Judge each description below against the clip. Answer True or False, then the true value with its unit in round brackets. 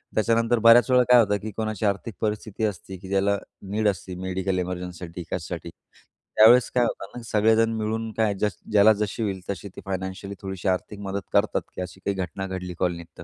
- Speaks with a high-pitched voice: False (100 Hz)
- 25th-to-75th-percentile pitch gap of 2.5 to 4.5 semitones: True (2.8 semitones)